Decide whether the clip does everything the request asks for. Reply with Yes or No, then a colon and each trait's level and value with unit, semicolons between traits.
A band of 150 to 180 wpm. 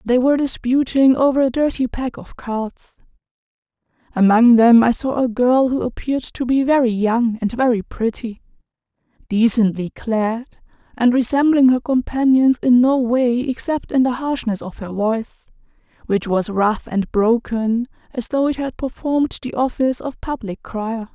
Yes: average, 155 wpm